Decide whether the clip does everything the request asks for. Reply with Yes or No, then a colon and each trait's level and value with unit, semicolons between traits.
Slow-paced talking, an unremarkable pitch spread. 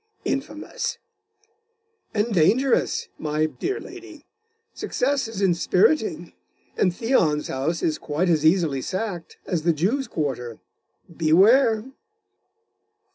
No: slow, 100 wpm; wide, 8.0 semitones